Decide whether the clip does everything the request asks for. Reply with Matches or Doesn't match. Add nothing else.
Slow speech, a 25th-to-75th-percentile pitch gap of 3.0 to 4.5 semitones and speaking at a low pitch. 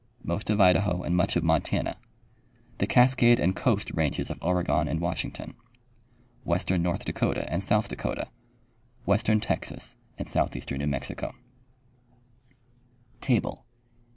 Matches